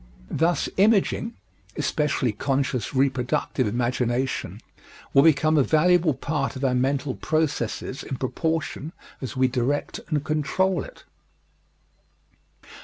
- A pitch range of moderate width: Yes, average, 3.4 semitones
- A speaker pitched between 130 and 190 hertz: Yes, medium, 140 Hz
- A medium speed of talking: No, slow, 110 wpm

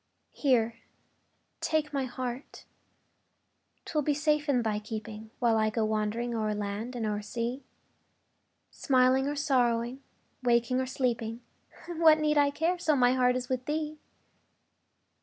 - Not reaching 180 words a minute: Yes, average, 140 wpm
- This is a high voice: Yes, very high, 250 Hz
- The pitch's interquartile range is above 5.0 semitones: No, average, 4.0 semitones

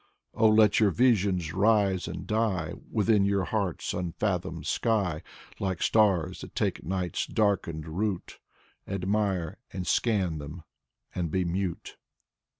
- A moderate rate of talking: No, slow, 125 wpm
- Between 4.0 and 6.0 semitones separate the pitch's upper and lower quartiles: No, average, 3.3 semitones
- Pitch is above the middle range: No, very low, 95 Hz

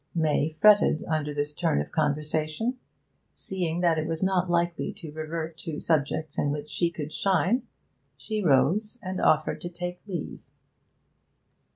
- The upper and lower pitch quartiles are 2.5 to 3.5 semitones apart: Yes, average, 2.8 semitones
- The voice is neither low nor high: Yes, medium, 160 Hz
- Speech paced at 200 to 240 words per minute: No, average, 155 wpm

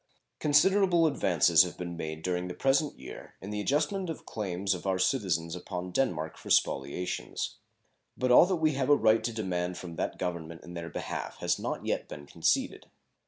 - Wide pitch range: Yes, wide, 7.7 semitones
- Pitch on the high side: No, very low, 95 Hz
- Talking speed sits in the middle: Yes, average, 185 wpm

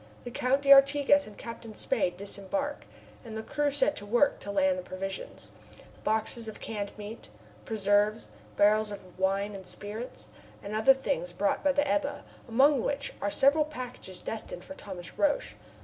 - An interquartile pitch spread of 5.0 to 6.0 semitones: Yes, wide, 5.4 semitones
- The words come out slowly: No, average, 165 wpm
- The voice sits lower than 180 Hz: No, high, 225 Hz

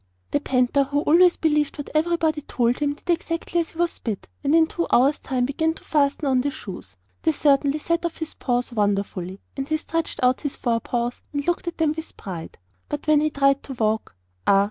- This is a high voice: Yes, very high, 285 Hz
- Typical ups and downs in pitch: Yes, average, 4.5 semitones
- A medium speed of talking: No, fast, 210 wpm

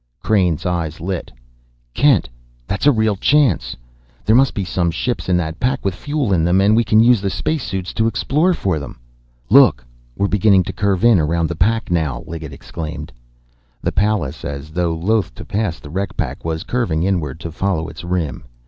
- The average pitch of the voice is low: Yes, very low, 95 Hz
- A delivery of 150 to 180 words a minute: No, average, 195 wpm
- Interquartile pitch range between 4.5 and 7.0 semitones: Yes, average, 5.1 semitones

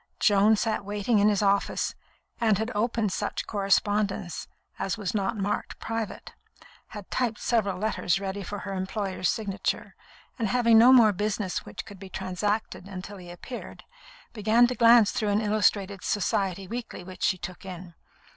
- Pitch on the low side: No, high, 205 Hz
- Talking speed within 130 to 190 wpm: Yes, average, 160 wpm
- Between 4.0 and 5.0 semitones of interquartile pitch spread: No, narrow, 2.4 semitones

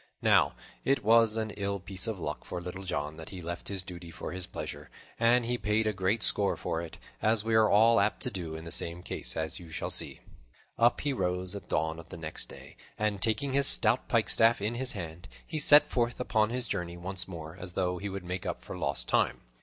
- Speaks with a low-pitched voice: Yes, very low, 95 Hz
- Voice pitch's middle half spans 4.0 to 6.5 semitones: Yes, average, 4.4 semitones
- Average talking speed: No, fast, 235 wpm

